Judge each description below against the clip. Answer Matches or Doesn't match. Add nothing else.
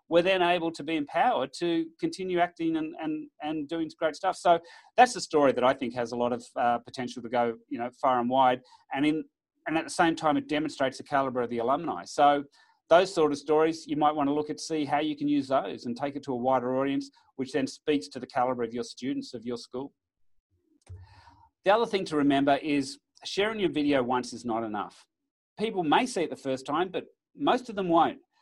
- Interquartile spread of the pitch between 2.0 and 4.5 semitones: Doesn't match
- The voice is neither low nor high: Matches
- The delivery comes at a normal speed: Doesn't match